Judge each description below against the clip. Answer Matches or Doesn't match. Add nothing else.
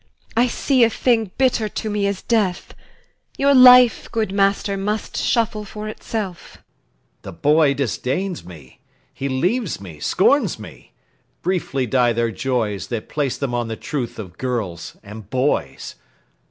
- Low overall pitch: Doesn't match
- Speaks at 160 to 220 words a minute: Doesn't match